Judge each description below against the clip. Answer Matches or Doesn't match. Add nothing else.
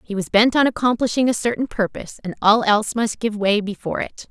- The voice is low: Doesn't match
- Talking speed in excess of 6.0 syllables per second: Matches